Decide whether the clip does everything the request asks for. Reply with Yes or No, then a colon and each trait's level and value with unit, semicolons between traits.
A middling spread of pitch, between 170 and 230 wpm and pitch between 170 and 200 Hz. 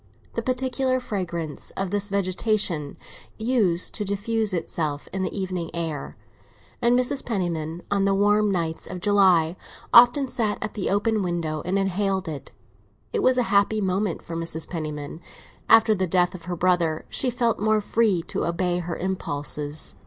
No: average, 4.2 semitones; average, 160 wpm; high, 190 Hz